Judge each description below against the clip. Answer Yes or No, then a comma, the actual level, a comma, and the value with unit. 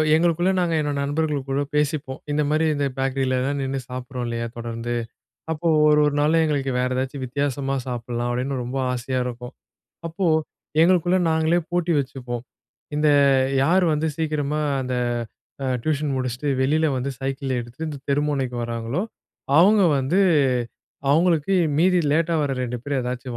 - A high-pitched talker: No, medium, 140 Hz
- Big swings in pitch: No, average, 3.8 semitones